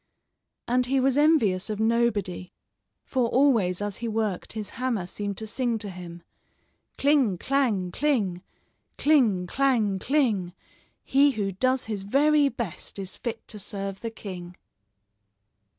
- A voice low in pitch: No, high, 220 Hz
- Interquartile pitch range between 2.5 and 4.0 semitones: No, average, 5.2 semitones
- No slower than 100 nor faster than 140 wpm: Yes, slow, 135 wpm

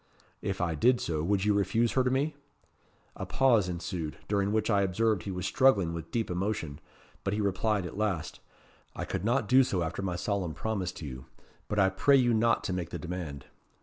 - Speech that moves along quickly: Yes, fast, 210 wpm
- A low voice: Yes, low, 100 Hz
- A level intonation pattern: No, average, 4.1 semitones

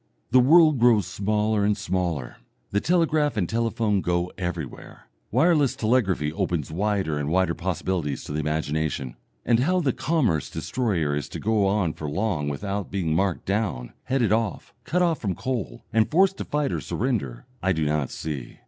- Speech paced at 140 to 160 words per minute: No, average, 170 wpm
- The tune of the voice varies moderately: No, wide, 7.0 semitones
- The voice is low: Yes, low, 100 Hz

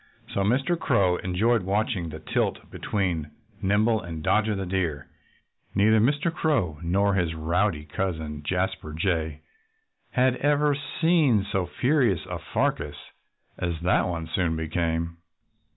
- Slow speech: Yes, slow, 130 wpm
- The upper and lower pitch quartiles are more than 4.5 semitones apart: Yes, average, 5.1 semitones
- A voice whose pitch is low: Yes, very low, 95 Hz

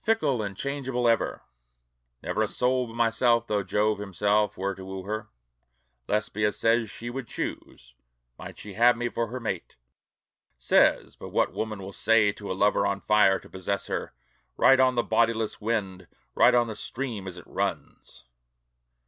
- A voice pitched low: Yes, low, 110 Hz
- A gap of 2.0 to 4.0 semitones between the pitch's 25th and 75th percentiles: Yes, average, 3.1 semitones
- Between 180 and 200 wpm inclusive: No, average, 170 wpm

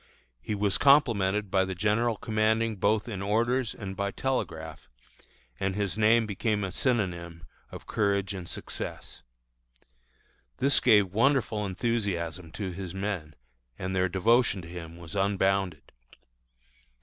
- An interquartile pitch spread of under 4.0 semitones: Yes, average, 3.0 semitones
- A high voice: No, low, 100 Hz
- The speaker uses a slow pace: Yes, slow, 130 wpm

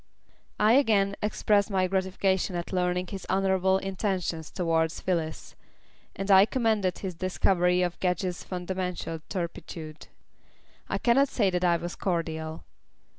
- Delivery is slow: Yes, slow, 125 wpm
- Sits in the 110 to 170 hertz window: No, medium, 185 Hz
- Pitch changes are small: Yes, narrow, 2.0 semitones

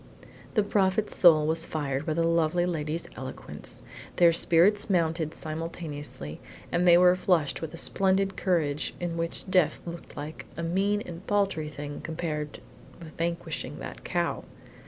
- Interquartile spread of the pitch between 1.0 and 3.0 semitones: Yes, narrow, 2.6 semitones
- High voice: No, medium, 170 Hz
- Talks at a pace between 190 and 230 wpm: No, average, 145 wpm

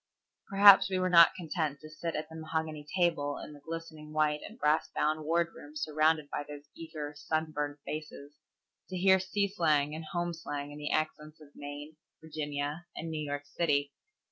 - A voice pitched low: No, medium, 155 Hz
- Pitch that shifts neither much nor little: No, narrow, 2.1 semitones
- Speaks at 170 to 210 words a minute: Yes, average, 175 wpm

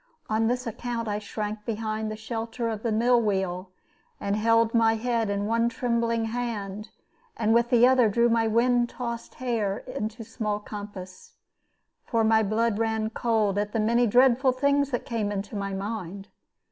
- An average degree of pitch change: No, narrow, 2.1 semitones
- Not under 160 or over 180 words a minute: Yes, average, 170 wpm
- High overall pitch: Yes, high, 225 Hz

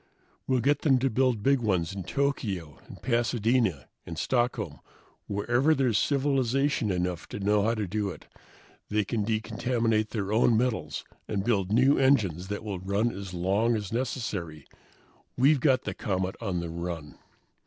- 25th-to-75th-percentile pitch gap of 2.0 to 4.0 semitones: No, average, 4.8 semitones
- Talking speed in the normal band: Yes, average, 160 wpm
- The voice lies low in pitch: Yes, low, 110 Hz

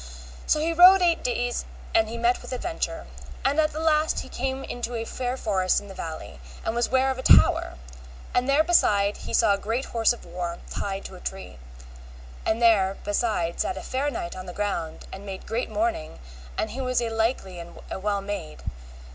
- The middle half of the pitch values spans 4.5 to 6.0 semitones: Yes, average, 5.3 semitones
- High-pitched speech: Yes, high, 230 Hz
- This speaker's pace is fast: Yes, fast, 210 wpm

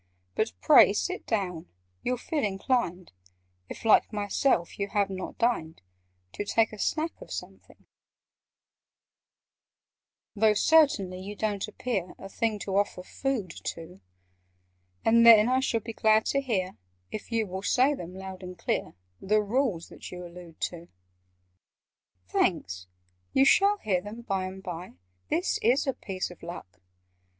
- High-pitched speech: Yes, high, 205 Hz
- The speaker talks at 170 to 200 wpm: No, average, 145 wpm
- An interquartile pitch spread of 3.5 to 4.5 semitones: Yes, average, 4.2 semitones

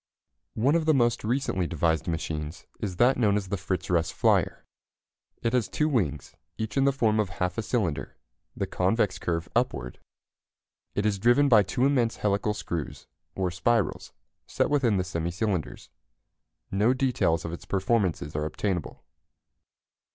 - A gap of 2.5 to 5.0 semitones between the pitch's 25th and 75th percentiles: No, wide, 5.5 semitones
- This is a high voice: No, low, 100 Hz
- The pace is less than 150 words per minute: No, average, 160 wpm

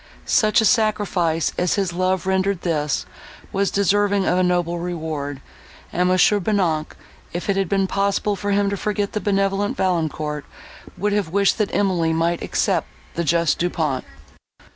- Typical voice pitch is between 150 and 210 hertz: Yes, medium, 185 Hz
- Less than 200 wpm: Yes, average, 165 wpm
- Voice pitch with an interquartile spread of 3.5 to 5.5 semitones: No, average, 3.1 semitones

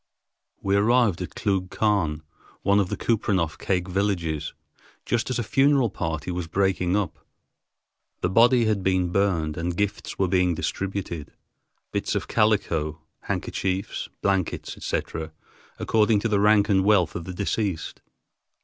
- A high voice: No, very low, 95 Hz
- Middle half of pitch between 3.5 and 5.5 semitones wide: No, average, 3.1 semitones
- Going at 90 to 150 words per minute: Yes, average, 140 wpm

